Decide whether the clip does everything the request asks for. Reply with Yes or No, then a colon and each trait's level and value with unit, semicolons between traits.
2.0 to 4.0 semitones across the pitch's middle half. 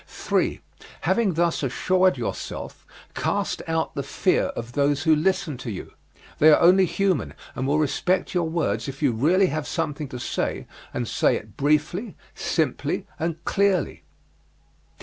No: average, 4.5 semitones